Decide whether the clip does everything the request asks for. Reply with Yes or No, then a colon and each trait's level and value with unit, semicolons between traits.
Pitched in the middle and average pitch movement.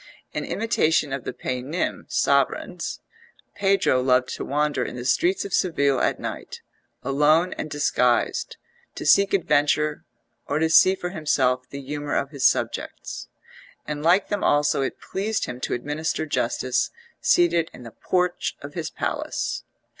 Yes: medium, 150 Hz; average, 4.4 semitones